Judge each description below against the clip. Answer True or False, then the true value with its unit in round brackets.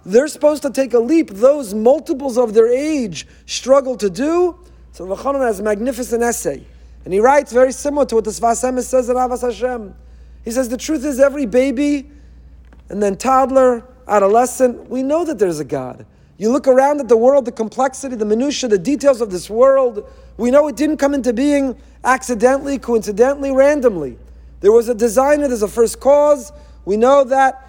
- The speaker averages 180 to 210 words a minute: True (185 wpm)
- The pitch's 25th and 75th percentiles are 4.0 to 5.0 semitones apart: False (3.3 semitones)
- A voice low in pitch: False (255 Hz)